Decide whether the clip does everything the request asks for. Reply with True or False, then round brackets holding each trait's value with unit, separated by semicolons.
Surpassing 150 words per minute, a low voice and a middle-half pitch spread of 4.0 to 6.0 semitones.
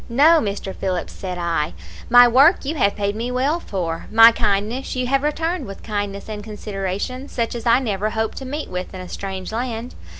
False (200 wpm; 220 Hz; 4.5 semitones)